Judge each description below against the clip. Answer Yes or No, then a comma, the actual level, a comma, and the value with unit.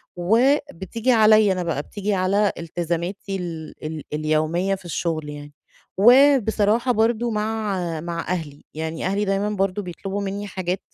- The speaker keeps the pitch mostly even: No, average, 4.1 semitones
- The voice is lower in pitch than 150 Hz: No, high, 195 Hz